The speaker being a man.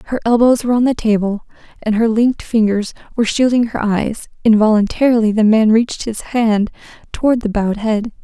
No: female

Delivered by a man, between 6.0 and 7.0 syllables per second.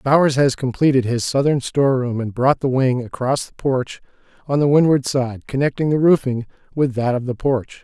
No: male; 5.1 syllables/s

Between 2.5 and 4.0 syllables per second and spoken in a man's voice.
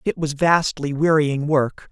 Yes: 3.9 syllables/s; male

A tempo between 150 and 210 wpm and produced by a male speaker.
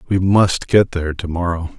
Yes: average, 200 wpm; male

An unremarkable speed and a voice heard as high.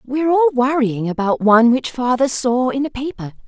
Yes: average, 190 wpm; very high, 255 Hz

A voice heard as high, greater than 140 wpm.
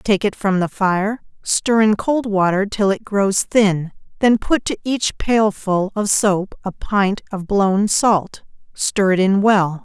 Yes: high, 200 Hz; average, 170 wpm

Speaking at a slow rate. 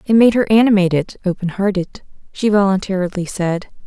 Yes: slow, 110 wpm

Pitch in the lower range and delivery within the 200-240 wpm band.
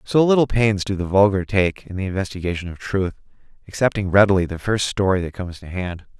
Yes: very low, 95 Hz; fast, 205 wpm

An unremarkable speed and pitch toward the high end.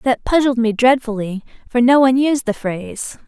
Yes: average, 185 wpm; high, 245 Hz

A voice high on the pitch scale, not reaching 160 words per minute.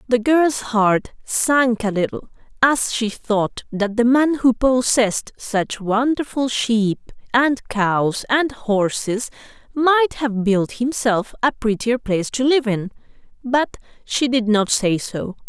Yes: high, 235 Hz; average, 145 wpm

